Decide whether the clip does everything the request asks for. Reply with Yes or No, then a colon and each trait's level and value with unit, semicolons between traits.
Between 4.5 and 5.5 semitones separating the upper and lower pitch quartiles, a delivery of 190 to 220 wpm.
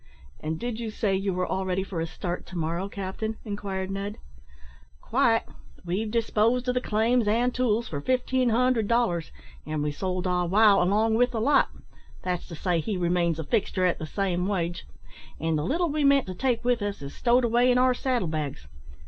Yes: average, 5.1 semitones; average, 200 wpm